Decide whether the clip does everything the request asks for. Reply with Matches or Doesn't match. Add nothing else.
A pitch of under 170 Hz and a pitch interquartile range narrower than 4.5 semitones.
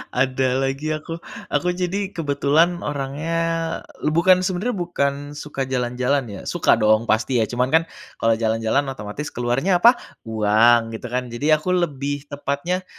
Doesn't match